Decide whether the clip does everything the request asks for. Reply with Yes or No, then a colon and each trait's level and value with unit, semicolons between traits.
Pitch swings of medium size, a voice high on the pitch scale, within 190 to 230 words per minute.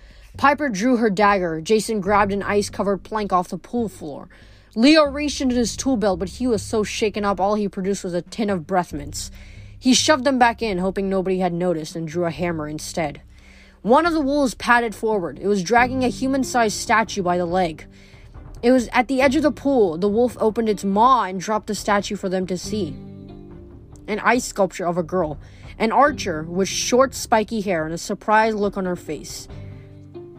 Yes: average, 4.8 semitones; high, 200 Hz; fast, 205 wpm